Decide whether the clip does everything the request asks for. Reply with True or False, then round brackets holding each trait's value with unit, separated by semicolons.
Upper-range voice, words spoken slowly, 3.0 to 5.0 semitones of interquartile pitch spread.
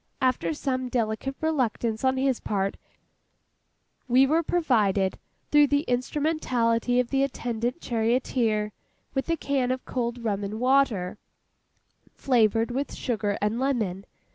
True (245 Hz; 125 wpm; 3.5 semitones)